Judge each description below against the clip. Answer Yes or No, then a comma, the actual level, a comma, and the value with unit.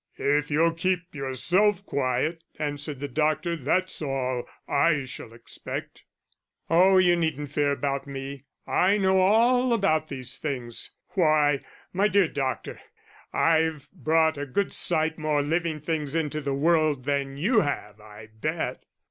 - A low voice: No, medium, 155 Hz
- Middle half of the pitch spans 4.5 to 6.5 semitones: No, average, 3.5 semitones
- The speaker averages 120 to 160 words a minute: Yes, average, 140 wpm